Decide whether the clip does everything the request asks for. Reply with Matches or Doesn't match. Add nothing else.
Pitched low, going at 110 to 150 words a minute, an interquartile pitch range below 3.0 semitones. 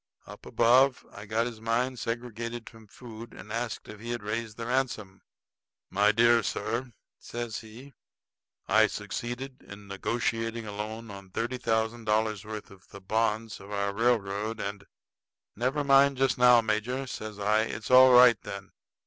Doesn't match